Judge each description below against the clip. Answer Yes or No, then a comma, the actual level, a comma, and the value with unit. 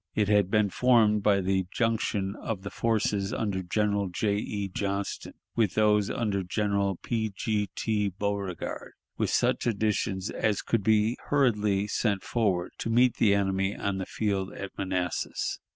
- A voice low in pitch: Yes, low, 100 Hz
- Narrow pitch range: Yes, narrow, 2.0 semitones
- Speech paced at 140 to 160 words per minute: Yes, average, 155 wpm